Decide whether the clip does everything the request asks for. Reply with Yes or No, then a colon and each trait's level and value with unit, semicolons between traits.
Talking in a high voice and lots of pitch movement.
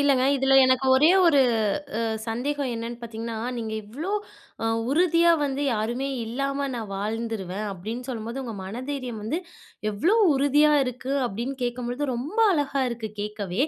No: high, 245 Hz; average, 3.7 semitones